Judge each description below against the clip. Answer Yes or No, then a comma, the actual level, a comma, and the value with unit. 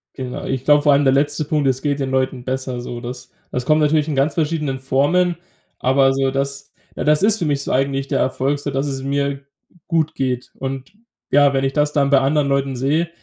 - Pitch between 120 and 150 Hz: Yes, medium, 140 Hz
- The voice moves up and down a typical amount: No, narrow, 1.8 semitones